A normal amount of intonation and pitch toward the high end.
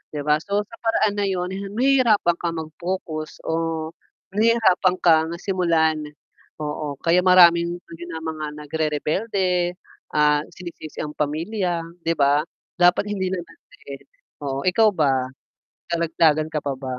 No: average, 3.5 semitones; medium, 170 Hz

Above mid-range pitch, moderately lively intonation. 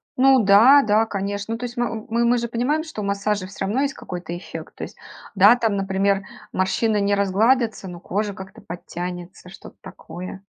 Yes: high, 205 Hz; average, 3.5 semitones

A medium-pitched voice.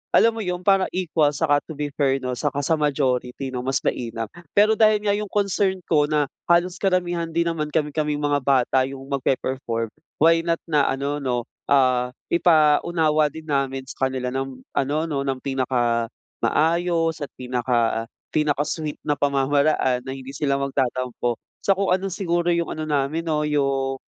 Yes: medium, 145 Hz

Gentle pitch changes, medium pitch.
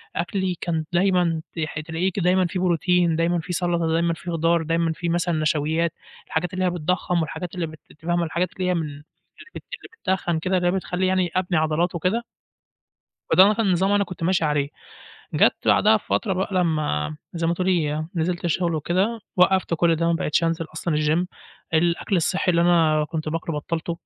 Yes: narrow, 2.1 semitones; medium, 170 Hz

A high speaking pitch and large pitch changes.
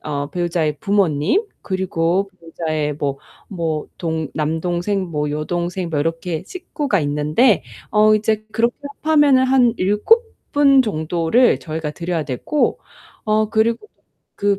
No: medium, 180 Hz; wide, 5.7 semitones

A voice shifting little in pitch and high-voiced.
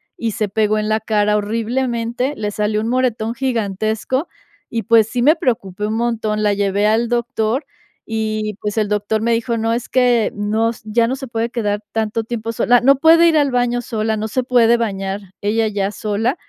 Yes: narrow, 2.2 semitones; high, 225 Hz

